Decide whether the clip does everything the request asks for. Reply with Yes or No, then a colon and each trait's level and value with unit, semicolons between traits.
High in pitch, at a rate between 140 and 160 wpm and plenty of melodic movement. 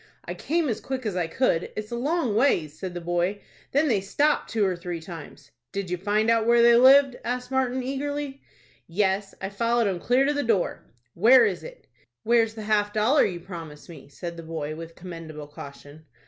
No: high, 210 Hz; fast, 205 wpm; wide, 6.4 semitones